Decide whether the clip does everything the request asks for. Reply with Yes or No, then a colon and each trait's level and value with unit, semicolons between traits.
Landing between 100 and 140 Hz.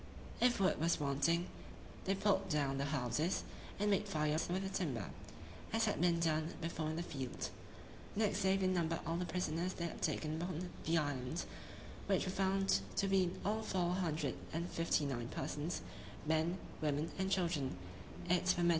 No: medium, 170 Hz